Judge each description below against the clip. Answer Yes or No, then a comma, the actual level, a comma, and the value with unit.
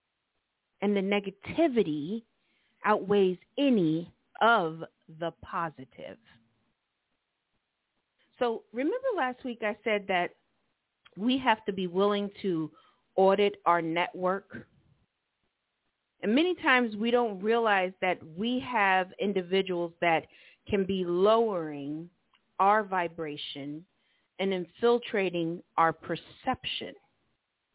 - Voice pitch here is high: Yes, high, 195 Hz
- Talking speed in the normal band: No, slow, 95 wpm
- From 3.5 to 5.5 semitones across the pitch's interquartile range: Yes, average, 4.7 semitones